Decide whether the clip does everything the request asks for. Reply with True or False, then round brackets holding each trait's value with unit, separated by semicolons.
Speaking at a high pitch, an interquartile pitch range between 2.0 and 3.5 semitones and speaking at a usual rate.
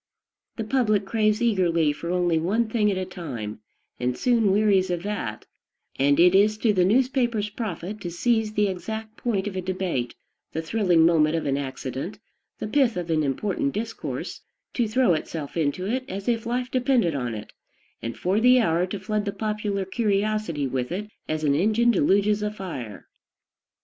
False (195 Hz; 4.7 semitones; 180 wpm)